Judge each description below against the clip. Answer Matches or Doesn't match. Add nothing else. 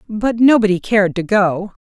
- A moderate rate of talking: Matches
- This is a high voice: Matches